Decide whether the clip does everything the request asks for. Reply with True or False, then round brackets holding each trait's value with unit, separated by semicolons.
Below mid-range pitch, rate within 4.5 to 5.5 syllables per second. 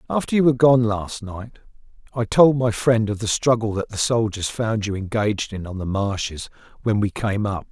True (110 Hz; 5.1 syllables/s)